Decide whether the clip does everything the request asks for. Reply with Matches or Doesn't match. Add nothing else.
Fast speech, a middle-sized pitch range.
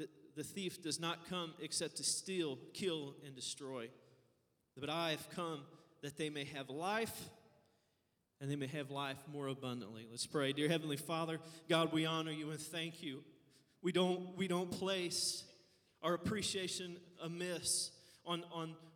Doesn't match